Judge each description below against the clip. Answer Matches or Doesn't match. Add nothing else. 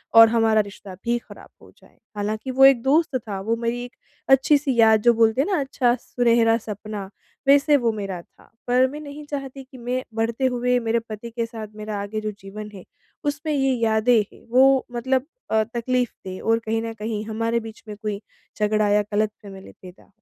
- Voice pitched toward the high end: Matches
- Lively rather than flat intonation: Doesn't match